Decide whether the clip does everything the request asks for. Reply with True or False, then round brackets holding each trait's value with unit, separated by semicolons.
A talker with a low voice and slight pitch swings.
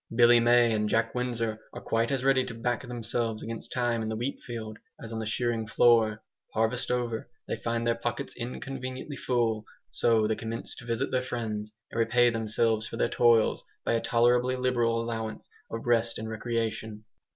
True (115 Hz; 1.5 semitones)